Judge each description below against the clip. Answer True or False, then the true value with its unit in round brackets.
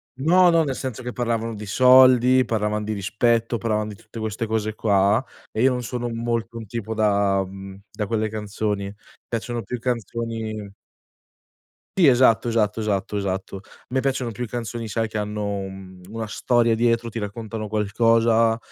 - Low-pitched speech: True (110 Hz)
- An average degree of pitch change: False (2.2 semitones)